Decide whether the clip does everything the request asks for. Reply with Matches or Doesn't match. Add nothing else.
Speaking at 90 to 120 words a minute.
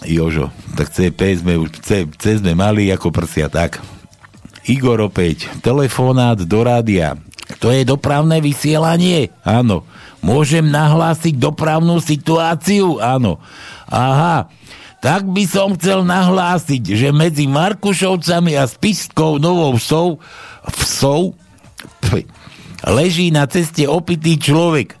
Matches